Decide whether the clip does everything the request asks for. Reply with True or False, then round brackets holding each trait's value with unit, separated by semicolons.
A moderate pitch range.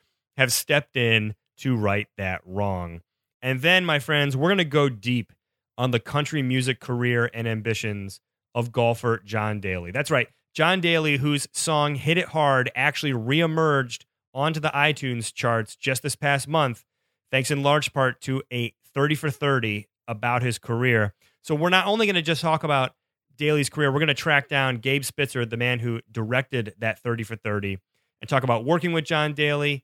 True (4.3 semitones)